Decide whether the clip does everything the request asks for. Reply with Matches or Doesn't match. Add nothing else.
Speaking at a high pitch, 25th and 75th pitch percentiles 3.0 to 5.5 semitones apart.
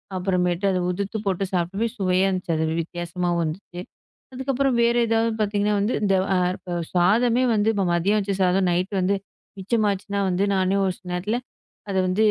Doesn't match